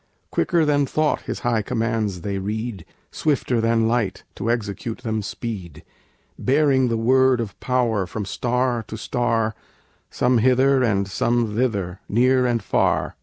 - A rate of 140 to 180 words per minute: Yes, average, 145 wpm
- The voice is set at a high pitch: No, low, 115 Hz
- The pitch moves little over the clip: No, average, 3.0 semitones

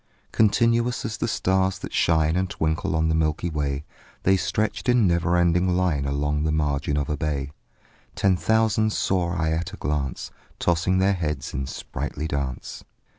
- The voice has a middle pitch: No, very low, 85 Hz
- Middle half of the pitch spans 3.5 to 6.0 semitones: Yes, average, 4.2 semitones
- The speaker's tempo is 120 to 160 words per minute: No, average, 170 wpm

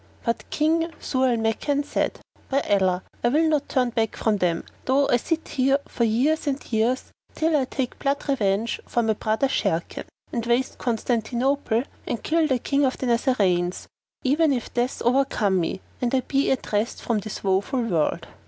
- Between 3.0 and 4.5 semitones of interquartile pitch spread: Yes, average, 4.0 semitones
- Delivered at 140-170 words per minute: No, average, 180 wpm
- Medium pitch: No, high, 245 Hz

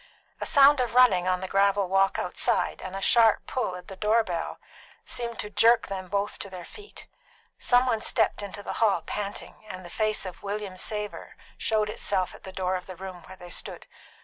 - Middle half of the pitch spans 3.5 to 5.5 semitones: No, average, 2.9 semitones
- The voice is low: No, high, 200 Hz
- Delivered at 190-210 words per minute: Yes, fast, 205 wpm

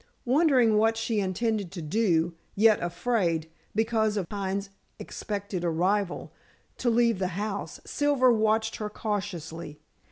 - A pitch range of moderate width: Yes, average, 3.6 semitones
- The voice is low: No, high, 210 Hz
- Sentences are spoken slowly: Yes, slow, 125 wpm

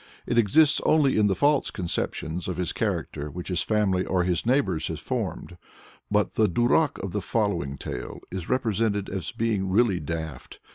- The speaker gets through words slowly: No, average, 175 wpm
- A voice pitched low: Yes, low, 100 Hz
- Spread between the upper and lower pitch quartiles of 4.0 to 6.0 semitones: Yes, average, 4.4 semitones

